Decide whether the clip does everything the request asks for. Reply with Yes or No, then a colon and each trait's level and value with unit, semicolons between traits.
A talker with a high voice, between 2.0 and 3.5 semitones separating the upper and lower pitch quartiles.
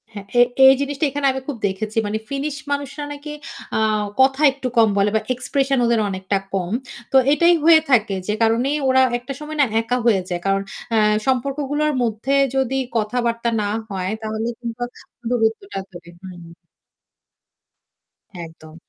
No: high, 240 Hz; average, 4.7 semitones